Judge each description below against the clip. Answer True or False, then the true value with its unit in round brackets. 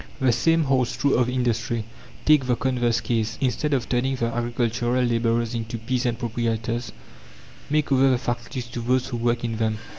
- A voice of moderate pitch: False (120 Hz)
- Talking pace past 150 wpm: True (175 wpm)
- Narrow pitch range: True (1.7 semitones)